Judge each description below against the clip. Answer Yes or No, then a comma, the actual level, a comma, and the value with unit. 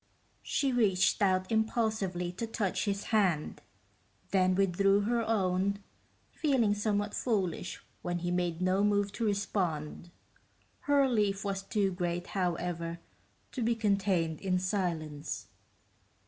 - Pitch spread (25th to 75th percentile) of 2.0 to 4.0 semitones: Yes, average, 3.1 semitones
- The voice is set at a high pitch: Yes, high, 195 Hz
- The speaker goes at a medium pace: No, slow, 120 wpm